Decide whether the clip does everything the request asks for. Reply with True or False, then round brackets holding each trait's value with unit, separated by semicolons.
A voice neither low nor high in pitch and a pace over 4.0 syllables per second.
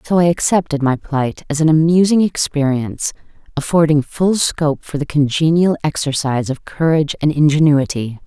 True (150 Hz; 5.3 syllables/s)